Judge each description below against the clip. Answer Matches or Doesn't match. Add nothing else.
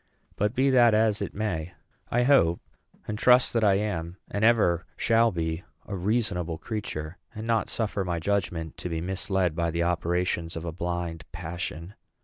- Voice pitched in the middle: Doesn't match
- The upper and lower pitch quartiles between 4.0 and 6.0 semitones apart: Matches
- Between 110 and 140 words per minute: Doesn't match